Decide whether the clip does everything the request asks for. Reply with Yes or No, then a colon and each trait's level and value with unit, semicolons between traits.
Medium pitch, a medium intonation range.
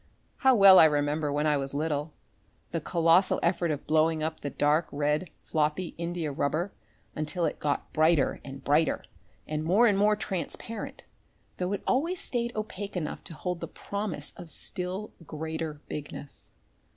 Yes: medium, 160 Hz; average, 3.9 semitones